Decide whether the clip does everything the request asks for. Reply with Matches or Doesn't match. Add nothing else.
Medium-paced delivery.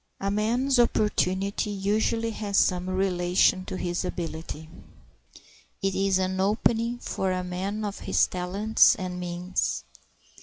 Doesn't match